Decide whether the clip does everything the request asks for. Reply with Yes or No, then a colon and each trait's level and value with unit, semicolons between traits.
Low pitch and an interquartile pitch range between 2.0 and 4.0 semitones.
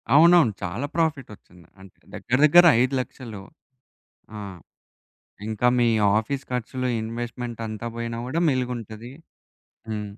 Yes: low, 120 Hz; average, 3.0 semitones